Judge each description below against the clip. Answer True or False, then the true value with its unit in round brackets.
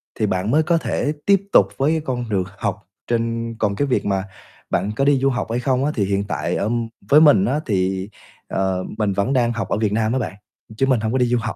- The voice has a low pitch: True (115 Hz)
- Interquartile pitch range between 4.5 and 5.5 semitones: True (5.0 semitones)